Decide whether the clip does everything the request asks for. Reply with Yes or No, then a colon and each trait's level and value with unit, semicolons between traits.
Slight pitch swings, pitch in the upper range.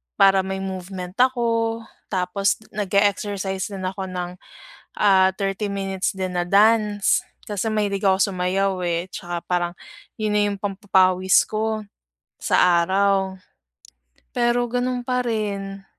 Yes: narrow, 2.1 semitones; high, 195 Hz